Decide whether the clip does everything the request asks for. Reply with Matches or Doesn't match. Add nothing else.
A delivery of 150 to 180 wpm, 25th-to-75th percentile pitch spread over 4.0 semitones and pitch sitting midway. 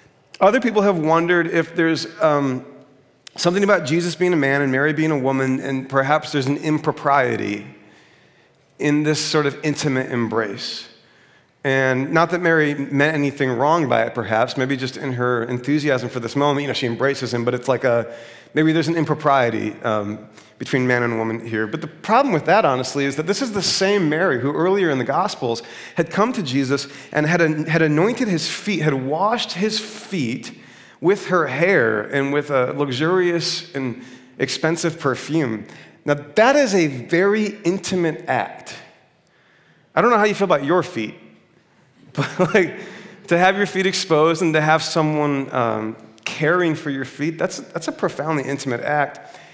Matches